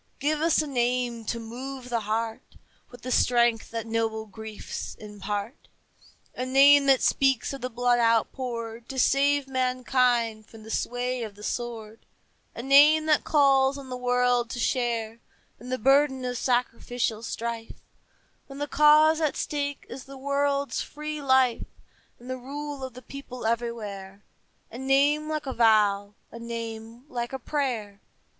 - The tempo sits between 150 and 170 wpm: Yes, average, 155 wpm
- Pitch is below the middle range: No, very high, 250 Hz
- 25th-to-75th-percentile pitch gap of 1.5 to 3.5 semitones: Yes, average, 3.2 semitones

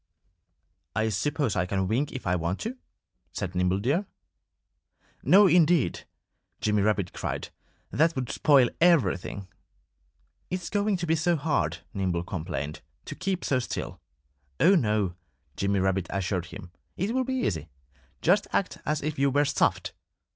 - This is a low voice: Yes, low, 125 Hz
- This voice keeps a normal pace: Yes, average, 145 wpm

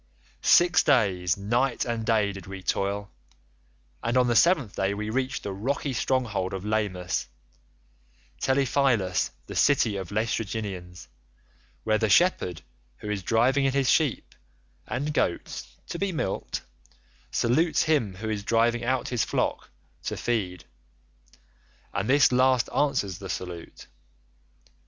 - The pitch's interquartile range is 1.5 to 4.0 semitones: No, average, 5.1 semitones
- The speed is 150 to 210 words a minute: No, slow, 135 wpm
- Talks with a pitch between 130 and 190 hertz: No, low, 110 Hz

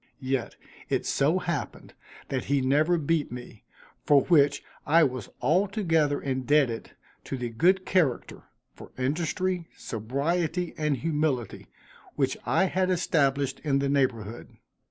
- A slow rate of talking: Yes, slow, 125 wpm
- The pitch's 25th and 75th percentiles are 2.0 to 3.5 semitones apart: No, average, 4.4 semitones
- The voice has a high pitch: No, medium, 145 Hz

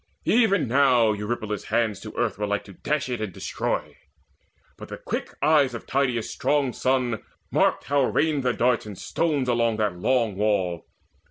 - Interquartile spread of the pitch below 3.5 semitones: No, average, 4.3 semitones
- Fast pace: No, average, 170 wpm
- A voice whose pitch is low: Yes, low, 120 Hz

